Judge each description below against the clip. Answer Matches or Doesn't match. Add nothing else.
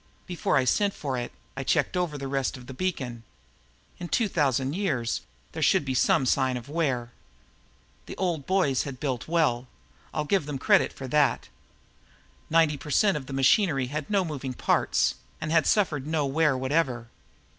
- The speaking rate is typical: Matches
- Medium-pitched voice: Matches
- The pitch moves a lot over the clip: Doesn't match